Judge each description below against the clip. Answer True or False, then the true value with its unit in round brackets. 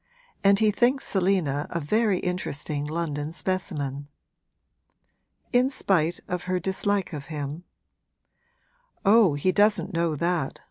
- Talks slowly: True (120 wpm)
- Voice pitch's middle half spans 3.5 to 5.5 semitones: True (4.9 semitones)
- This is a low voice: False (180 Hz)